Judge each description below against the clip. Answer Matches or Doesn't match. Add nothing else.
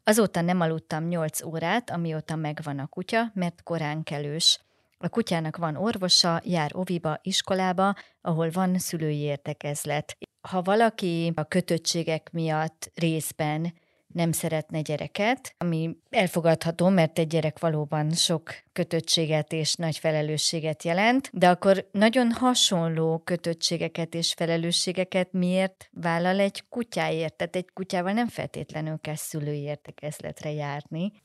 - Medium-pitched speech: Matches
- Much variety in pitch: Doesn't match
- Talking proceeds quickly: Doesn't match